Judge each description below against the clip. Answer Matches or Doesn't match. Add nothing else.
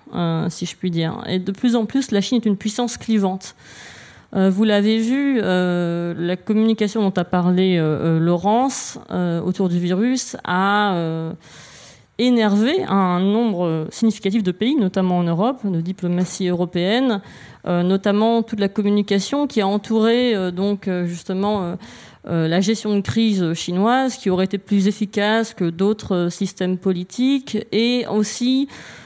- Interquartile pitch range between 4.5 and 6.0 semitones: Doesn't match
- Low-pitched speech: Doesn't match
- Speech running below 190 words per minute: Matches